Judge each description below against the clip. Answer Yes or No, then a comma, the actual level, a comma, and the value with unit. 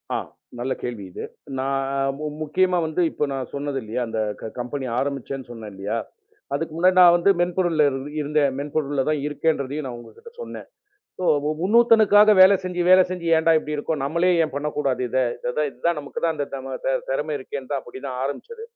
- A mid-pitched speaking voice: Yes, medium, 145 Hz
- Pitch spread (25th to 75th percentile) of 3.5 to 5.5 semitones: Yes, average, 4.4 semitones